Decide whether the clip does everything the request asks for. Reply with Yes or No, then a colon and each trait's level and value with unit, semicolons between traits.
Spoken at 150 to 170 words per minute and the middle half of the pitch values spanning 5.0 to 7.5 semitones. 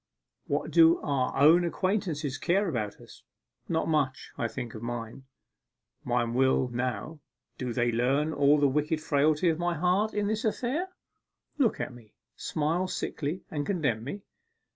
Yes: average, 155 wpm; wide, 5.5 semitones